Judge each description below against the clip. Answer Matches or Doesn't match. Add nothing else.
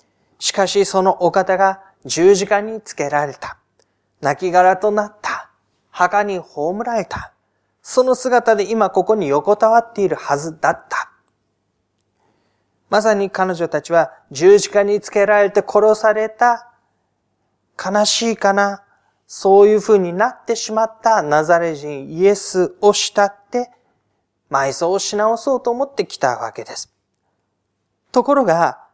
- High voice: Matches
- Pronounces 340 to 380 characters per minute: Doesn't match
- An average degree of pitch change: Matches